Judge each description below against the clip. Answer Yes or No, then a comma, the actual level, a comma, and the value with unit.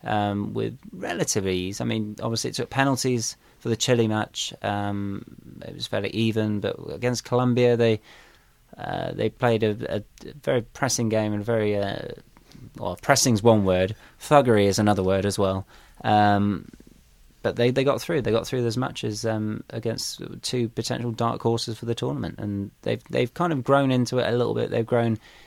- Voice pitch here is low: Yes, low, 115 Hz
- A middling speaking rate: Yes, average, 185 wpm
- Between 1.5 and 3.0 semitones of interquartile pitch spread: Yes, average, 2.7 semitones